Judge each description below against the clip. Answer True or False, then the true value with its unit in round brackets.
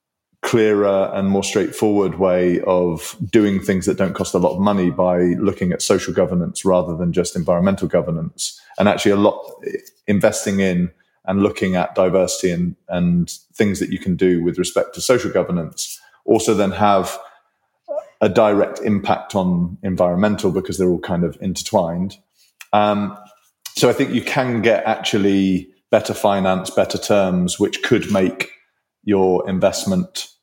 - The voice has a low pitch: True (95 Hz)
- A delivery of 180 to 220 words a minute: False (155 wpm)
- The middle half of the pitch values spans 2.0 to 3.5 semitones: True (2.7 semitones)